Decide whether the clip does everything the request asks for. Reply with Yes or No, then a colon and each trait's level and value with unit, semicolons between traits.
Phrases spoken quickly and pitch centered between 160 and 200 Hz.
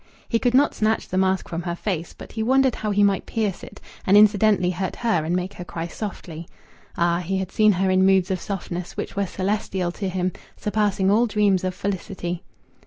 Yes: fast, 210 wpm; high, 190 Hz